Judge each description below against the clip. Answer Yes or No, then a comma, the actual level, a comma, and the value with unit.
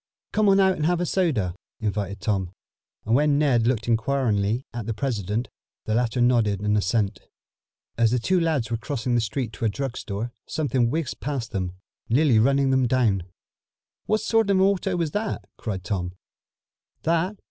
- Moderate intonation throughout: No, wide, 6.0 semitones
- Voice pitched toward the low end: Yes, low, 120 Hz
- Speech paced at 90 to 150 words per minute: No, average, 180 wpm